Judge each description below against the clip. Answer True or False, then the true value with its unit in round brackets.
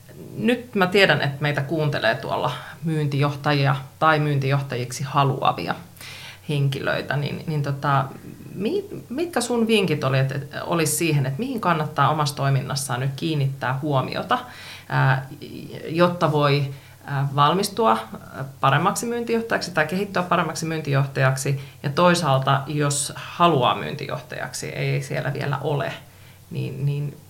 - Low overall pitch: False (145 Hz)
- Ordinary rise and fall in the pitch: True (3.3 semitones)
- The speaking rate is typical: True (110 wpm)